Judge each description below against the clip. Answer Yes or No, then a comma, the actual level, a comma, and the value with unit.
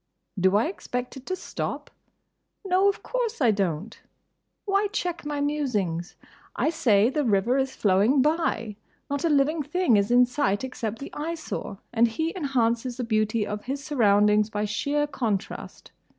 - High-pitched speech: Yes, very high, 250 Hz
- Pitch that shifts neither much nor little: No, wide, 5.9 semitones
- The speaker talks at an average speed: Yes, average, 160 wpm